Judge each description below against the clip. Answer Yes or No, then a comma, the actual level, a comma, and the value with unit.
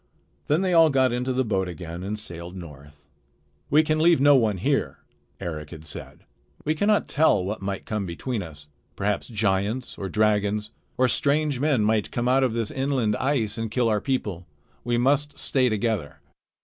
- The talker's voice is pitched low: Yes, low, 110 Hz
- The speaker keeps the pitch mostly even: No, wide, 5.6 semitones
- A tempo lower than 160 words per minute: No, average, 180 wpm